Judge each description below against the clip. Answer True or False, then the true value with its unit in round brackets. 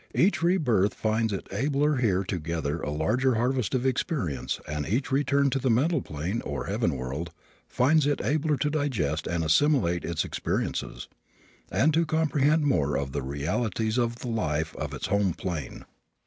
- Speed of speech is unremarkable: True (170 wpm)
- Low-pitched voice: True (115 Hz)